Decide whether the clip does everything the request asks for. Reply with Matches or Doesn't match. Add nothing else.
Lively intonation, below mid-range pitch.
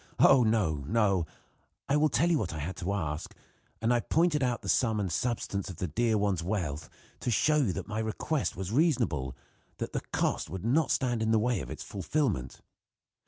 Matches